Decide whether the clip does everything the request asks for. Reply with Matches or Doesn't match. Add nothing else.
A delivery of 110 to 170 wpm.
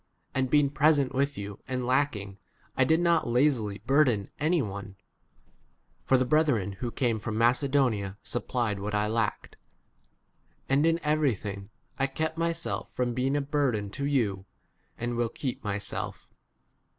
Matches